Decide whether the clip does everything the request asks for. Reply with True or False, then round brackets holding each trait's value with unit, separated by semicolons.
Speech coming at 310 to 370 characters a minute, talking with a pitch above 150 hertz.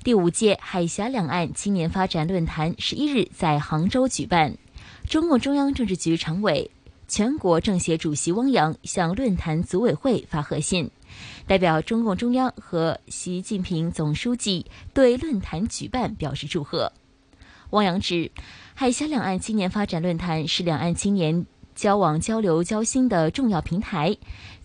False (240 characters per minute; 185 Hz)